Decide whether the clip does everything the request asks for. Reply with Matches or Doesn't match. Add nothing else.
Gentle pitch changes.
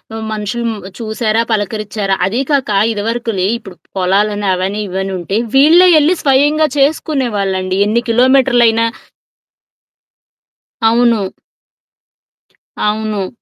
Doesn't match